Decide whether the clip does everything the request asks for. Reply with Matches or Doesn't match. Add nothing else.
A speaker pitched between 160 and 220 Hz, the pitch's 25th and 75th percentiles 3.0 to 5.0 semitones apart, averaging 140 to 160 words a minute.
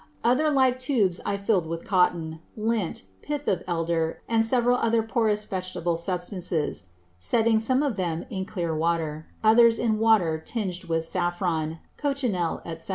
Doesn't match